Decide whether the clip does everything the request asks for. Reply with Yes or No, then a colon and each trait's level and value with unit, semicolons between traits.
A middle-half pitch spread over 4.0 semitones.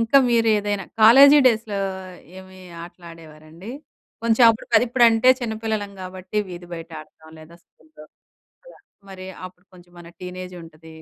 Yes: average, 4.8 semitones